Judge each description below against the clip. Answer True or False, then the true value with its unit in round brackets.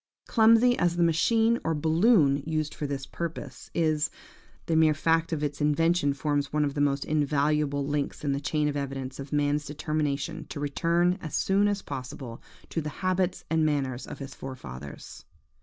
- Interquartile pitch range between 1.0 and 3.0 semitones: True (2.7 semitones)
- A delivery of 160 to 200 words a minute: True (175 wpm)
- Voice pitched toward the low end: False (150 Hz)